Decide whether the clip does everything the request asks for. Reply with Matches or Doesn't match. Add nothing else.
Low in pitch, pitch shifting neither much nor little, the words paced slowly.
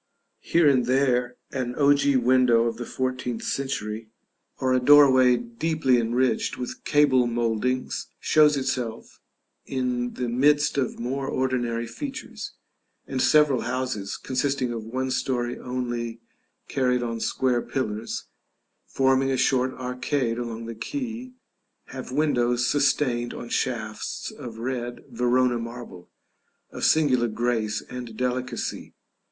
Doesn't match